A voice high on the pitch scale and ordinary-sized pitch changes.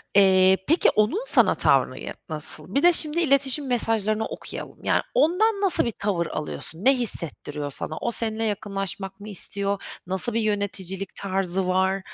Yes: high, 200 Hz; average, 4.4 semitones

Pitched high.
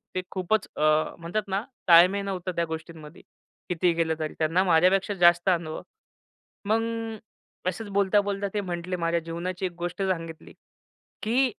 No: medium, 180 Hz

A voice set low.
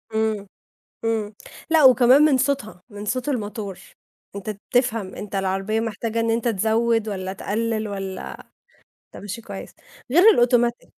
No: high, 220 Hz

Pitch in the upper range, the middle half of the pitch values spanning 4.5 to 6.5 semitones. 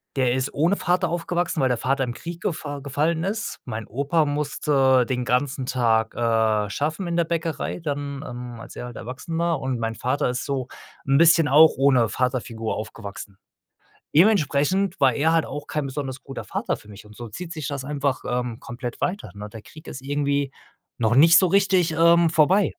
No: medium, 140 Hz; average, 4.8 semitones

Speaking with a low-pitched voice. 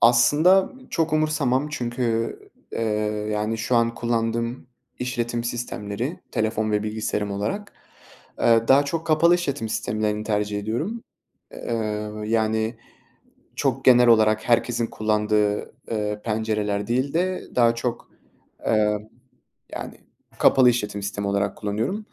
Yes: low, 115 Hz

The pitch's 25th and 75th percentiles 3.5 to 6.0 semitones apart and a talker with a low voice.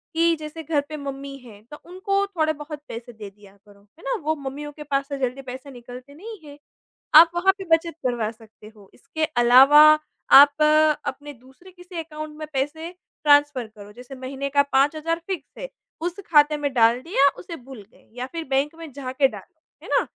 No: average, 4.0 semitones; very high, 285 Hz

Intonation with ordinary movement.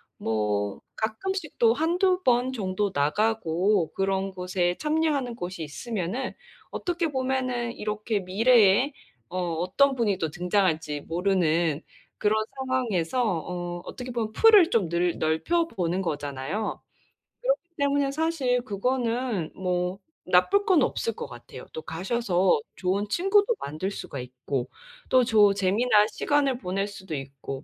No: wide, 6.5 semitones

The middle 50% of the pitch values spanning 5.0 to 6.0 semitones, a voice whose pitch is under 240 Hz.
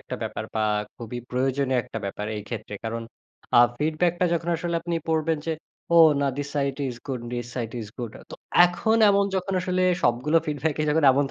Yes: wide, 5.4 semitones; medium, 140 Hz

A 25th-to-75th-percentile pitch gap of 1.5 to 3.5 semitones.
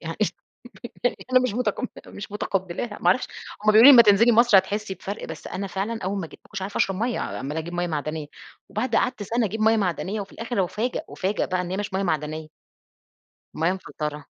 No: average, 4.0 semitones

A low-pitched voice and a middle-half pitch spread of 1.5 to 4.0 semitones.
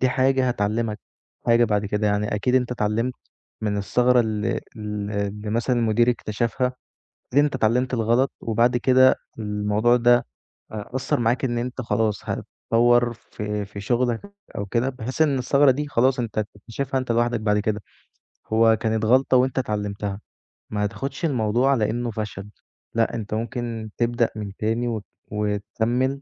Yes: low, 115 Hz; average, 2.9 semitones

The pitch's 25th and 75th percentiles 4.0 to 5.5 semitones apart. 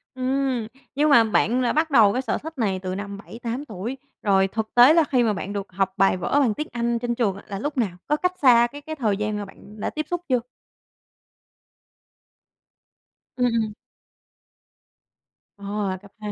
Yes: average, 4.7 semitones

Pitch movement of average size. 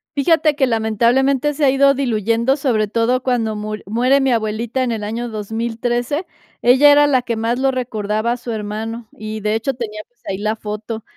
Yes: average, 3.4 semitones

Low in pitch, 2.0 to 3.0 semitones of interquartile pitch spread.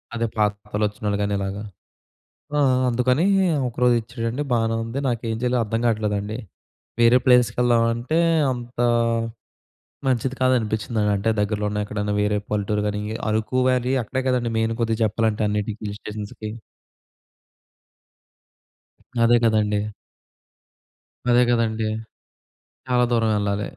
Yes: low, 115 Hz; narrow, 2.5 semitones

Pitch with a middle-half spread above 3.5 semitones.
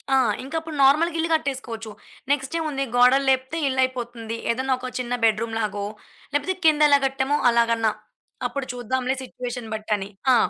No: average, 3.2 semitones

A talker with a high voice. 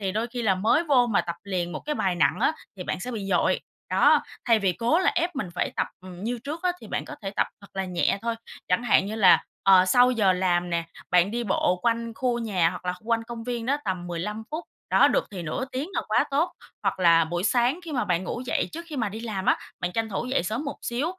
Yes: high, 220 Hz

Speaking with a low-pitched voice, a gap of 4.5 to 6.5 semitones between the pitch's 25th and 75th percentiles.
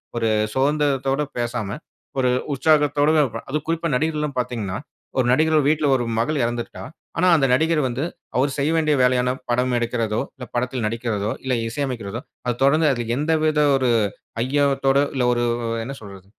No: low, 130 Hz; average, 3.7 semitones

